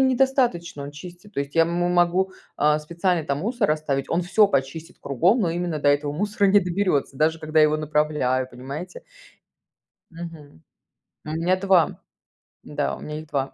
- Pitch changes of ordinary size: Yes, average, 3.6 semitones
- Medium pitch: Yes, medium, 165 Hz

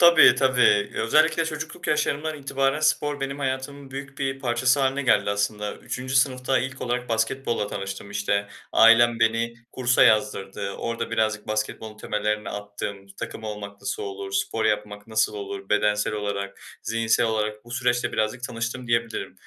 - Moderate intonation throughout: Yes, average, 3.8 semitones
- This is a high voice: No, low, 115 Hz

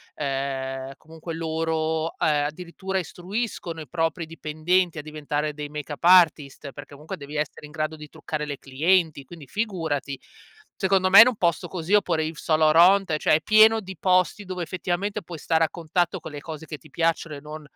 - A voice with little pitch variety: No, average, 3.1 semitones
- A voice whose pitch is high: No, medium, 160 Hz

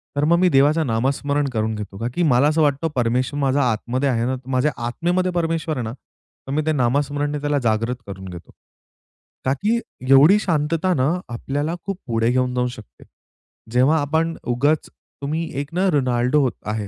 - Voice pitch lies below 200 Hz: Yes, medium, 140 Hz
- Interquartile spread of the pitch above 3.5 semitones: Yes, average, 4.1 semitones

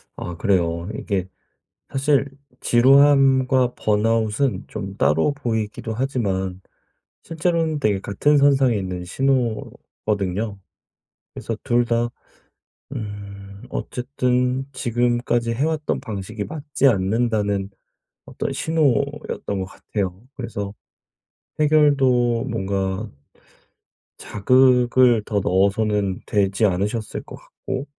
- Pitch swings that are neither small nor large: Yes, average, 4.9 semitones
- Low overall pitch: Yes, low, 115 Hz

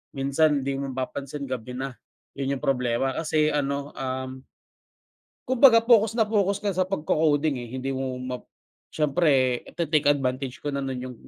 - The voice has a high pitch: No, medium, 140 Hz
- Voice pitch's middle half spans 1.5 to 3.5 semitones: Yes, average, 3.2 semitones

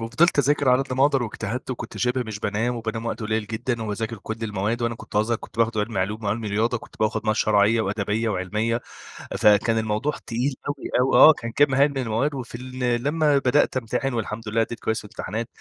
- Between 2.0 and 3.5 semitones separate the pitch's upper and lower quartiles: Yes, average, 2.8 semitones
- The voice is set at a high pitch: No, low, 115 Hz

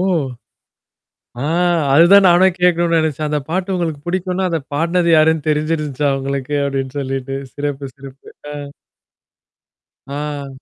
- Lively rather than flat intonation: No, average, 3.6 semitones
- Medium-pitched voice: Yes, medium, 150 Hz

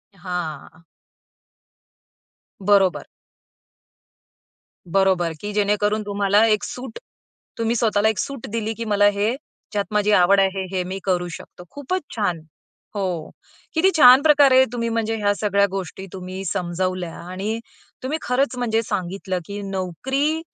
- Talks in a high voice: Yes, high, 205 Hz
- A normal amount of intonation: Yes, average, 3.6 semitones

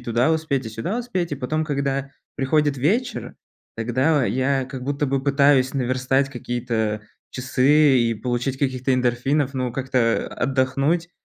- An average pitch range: No, narrow, 2.3 semitones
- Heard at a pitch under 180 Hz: Yes, low, 135 Hz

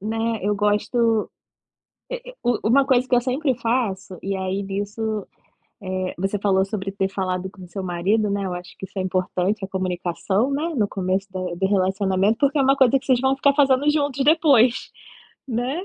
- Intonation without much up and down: No, average, 5.0 semitones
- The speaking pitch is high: Yes, high, 205 Hz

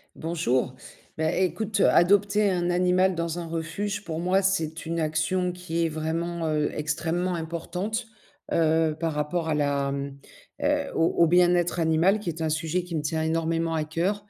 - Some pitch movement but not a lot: No, narrow, 2.3 semitones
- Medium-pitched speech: Yes, medium, 165 Hz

